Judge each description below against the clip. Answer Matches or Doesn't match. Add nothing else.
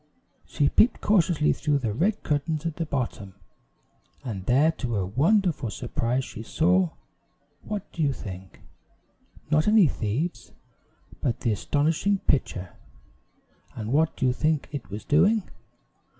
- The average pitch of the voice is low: Doesn't match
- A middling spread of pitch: Doesn't match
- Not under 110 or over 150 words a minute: Matches